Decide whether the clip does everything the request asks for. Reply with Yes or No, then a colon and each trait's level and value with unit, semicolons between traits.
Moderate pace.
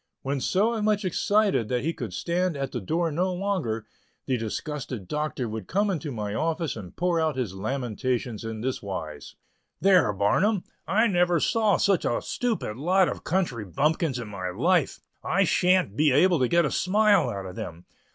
Yes: average, 180 wpm